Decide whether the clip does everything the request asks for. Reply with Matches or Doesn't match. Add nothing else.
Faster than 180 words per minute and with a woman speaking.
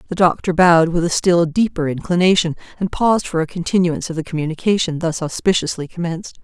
Doesn't match